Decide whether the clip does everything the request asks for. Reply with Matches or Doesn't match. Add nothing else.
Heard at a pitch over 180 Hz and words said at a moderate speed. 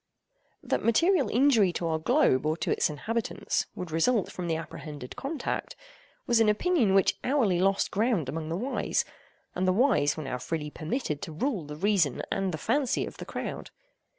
Matches